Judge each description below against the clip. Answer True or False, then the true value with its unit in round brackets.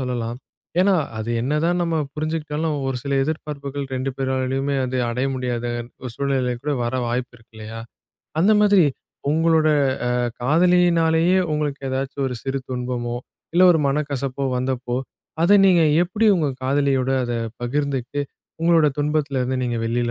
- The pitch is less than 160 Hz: True (140 Hz)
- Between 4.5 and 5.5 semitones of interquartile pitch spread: False (3.9 semitones)